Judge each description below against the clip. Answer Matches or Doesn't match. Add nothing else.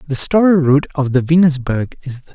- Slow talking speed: Doesn't match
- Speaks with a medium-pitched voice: Matches